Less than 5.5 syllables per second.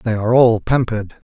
No: 6.4 syllables/s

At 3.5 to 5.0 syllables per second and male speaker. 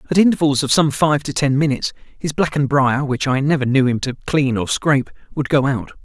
Yes: 4.4 syllables/s; male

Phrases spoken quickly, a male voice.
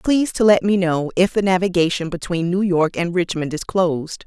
No: fast, 210 wpm; female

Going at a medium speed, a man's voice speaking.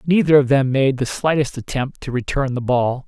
No: fast, 215 wpm; male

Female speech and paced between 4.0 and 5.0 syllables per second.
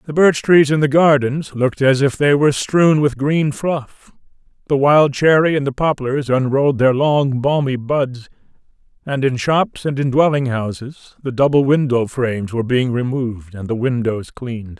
No: male; 4.6 syllables/s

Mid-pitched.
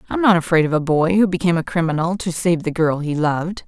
Yes: medium, 170 Hz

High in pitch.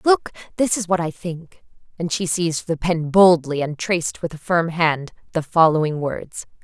No: medium, 170 Hz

